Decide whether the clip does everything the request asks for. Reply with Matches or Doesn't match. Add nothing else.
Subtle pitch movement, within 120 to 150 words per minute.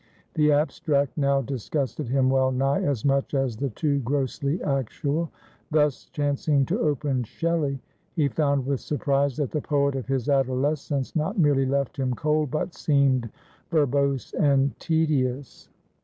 Matches